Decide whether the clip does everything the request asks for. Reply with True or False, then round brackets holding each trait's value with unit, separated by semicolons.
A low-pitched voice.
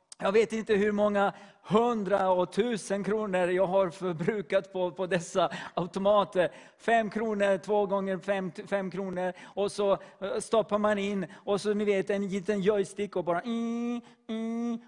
False (200 Hz)